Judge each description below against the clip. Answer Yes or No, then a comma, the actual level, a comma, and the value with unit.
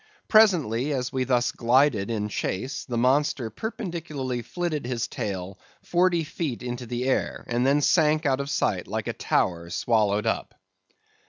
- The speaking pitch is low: Yes, low, 130 Hz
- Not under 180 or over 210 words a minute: No, average, 155 wpm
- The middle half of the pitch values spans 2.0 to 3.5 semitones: No, average, 4.5 semitones